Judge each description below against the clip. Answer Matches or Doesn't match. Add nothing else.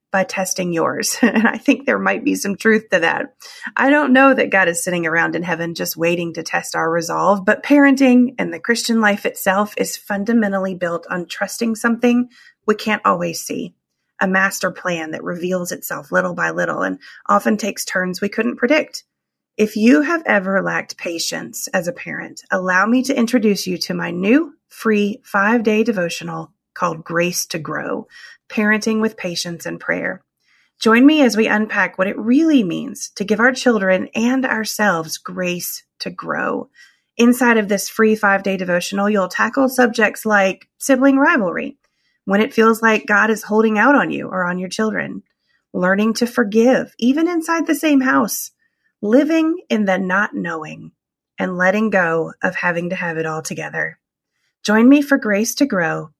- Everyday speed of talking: Matches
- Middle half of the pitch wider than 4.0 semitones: Matches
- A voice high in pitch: Matches